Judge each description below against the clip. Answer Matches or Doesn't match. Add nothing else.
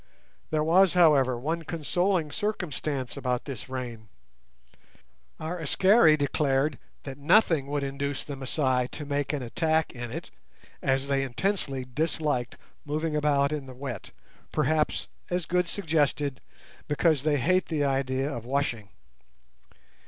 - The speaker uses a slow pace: Matches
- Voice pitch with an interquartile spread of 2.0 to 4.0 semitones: Matches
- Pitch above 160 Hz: Doesn't match